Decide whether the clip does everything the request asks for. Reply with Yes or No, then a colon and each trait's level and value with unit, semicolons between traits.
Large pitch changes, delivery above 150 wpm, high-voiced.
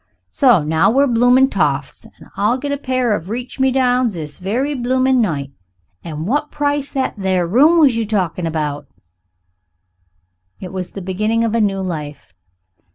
Yes: wide, 6.5 semitones; average, 165 wpm; high, 225 Hz